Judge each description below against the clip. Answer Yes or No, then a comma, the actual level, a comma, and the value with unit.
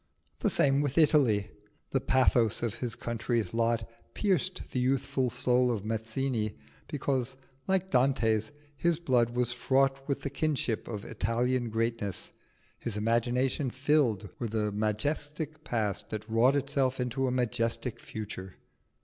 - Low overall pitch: Yes, low, 125 Hz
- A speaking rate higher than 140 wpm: No, slow, 135 wpm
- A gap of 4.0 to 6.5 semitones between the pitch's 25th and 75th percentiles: No, average, 3.3 semitones